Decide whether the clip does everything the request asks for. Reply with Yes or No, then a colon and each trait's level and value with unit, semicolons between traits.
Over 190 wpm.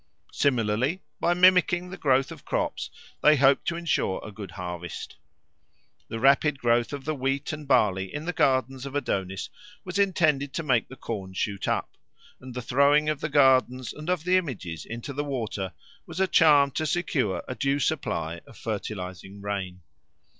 No: average, 175 wpm